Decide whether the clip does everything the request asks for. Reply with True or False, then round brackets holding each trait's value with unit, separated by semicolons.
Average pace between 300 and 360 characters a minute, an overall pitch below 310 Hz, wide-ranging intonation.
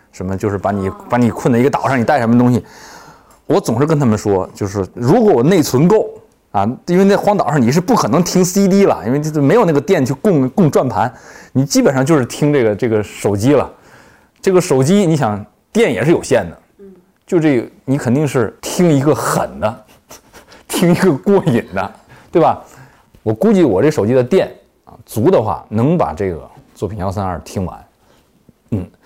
False (275 characters per minute; 135 Hz; 7.4 semitones)